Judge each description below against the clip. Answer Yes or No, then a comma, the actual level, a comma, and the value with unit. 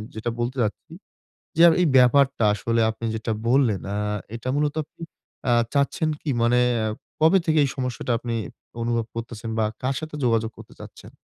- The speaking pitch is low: Yes, low, 125 Hz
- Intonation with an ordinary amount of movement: Yes, average, 3.5 semitones